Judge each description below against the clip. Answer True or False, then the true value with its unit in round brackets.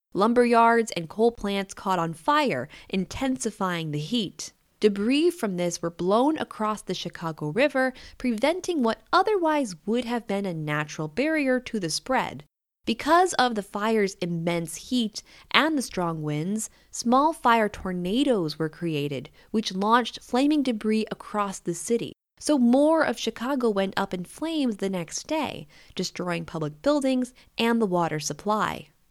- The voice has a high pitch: True (220 Hz)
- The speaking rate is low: False (150 wpm)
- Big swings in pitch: True (6.3 semitones)